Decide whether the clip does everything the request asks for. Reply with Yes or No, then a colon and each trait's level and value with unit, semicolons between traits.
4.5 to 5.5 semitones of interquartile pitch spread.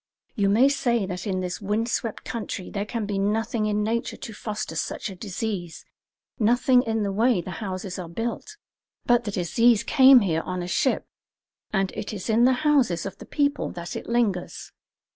No: average, 4.0 semitones